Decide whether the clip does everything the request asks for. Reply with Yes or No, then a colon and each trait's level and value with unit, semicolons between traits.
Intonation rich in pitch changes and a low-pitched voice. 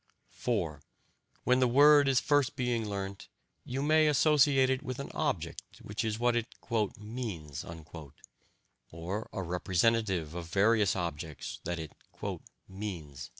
Yes: wide, 6.6 semitones; low, 110 Hz